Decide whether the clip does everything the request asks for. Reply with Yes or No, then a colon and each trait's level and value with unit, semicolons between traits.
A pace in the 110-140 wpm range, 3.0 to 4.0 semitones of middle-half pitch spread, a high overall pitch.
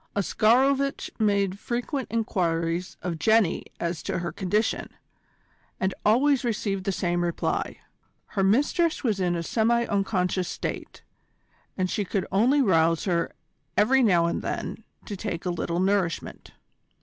No: slow, 135 wpm; average, 4.4 semitones; high, 195 Hz